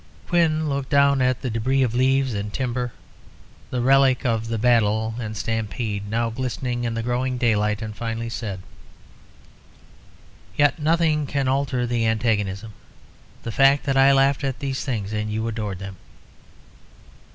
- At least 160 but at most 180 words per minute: No, average, 150 wpm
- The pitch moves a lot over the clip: No, average, 3.4 semitones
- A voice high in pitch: No, low, 120 Hz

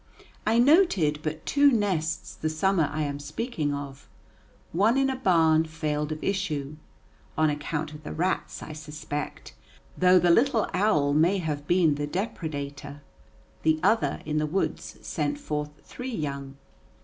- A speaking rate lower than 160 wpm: Yes, average, 150 wpm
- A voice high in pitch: No, medium, 155 Hz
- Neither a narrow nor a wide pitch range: Yes, average, 4.6 semitones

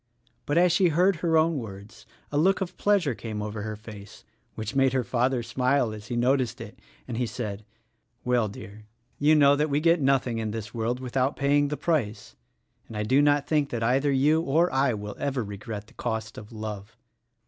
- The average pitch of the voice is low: Yes, low, 125 Hz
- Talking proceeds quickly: Yes, fast, 210 wpm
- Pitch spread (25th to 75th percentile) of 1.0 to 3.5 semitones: No, average, 4.9 semitones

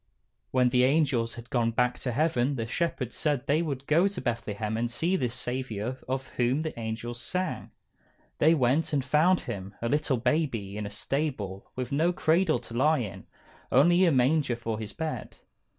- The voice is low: Yes, low, 130 Hz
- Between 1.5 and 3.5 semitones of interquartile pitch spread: No, average, 4.8 semitones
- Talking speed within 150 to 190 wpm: Yes, average, 185 wpm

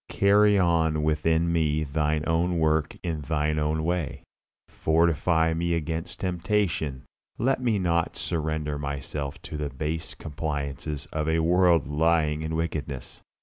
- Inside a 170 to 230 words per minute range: No, slow, 135 wpm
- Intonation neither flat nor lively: No, narrow, 1.9 semitones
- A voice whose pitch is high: No, very low, 80 Hz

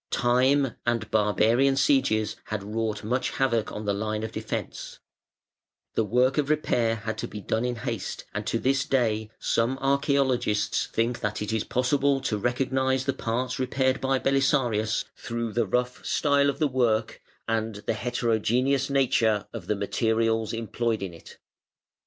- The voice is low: Yes, low, 120 Hz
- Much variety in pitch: No, average, 3.3 semitones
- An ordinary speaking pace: Yes, average, 160 wpm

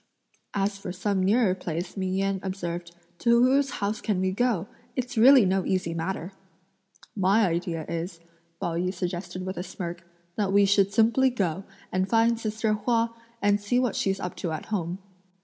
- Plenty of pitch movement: No, average, 3.4 semitones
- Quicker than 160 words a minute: Yes, average, 175 wpm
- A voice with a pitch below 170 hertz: No, high, 195 Hz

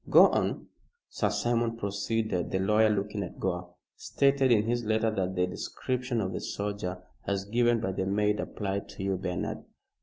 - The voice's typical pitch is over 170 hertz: No, low, 105 Hz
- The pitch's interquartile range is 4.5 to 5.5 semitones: No, average, 3.1 semitones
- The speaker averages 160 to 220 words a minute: Yes, average, 175 wpm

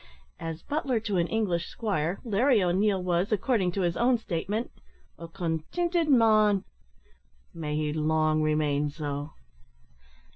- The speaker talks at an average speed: No, slow, 125 wpm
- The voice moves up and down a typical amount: No, wide, 5.8 semitones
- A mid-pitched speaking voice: Yes, medium, 180 Hz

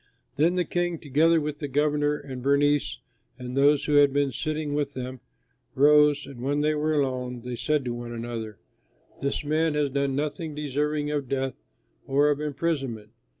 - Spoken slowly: No, average, 175 wpm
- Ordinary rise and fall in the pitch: No, narrow, 2.1 semitones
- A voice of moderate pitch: Yes, medium, 145 Hz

